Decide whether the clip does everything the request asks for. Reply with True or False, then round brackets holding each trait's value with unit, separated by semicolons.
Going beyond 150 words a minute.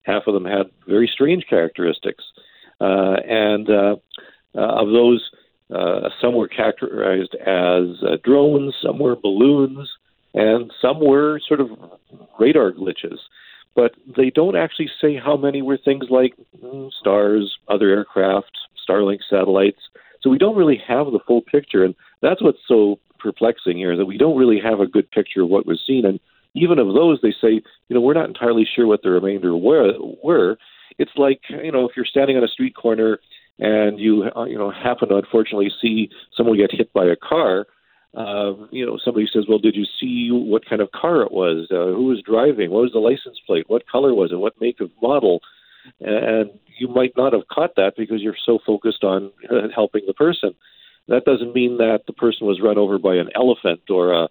True (195 wpm)